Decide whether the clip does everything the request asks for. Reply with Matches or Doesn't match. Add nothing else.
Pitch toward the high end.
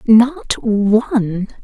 Matches